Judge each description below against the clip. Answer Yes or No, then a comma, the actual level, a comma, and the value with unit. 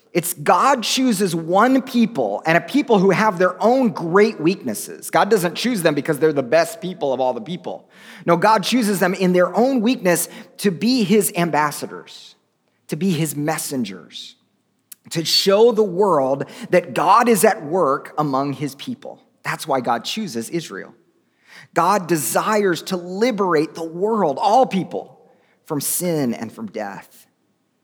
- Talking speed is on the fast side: No, average, 155 wpm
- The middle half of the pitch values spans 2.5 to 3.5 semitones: No, average, 5.1 semitones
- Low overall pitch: No, medium, 185 Hz